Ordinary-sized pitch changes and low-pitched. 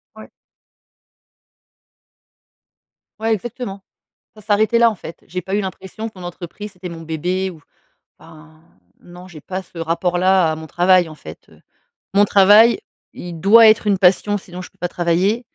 No: average, 3.1 semitones; medium, 185 Hz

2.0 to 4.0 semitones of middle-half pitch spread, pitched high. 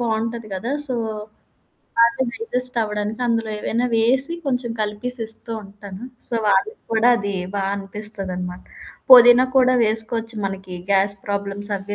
Yes: average, 3.2 semitones; high, 220 Hz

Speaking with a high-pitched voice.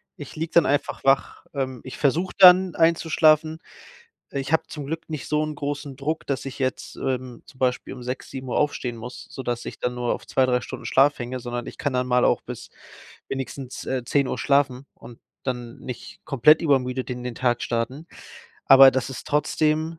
No: low, 135 Hz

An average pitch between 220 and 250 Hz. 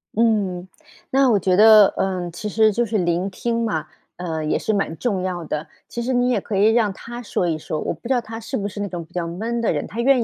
No: high, 205 Hz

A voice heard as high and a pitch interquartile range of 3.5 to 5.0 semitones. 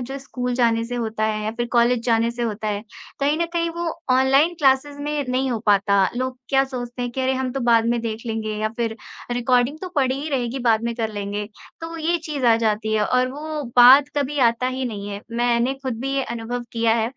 No: high, 245 Hz; average, 2.9 semitones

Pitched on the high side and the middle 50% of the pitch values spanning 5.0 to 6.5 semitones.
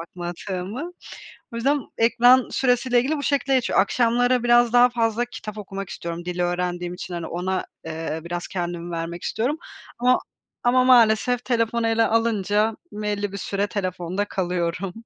Yes: high, 210 Hz; wide, 5.4 semitones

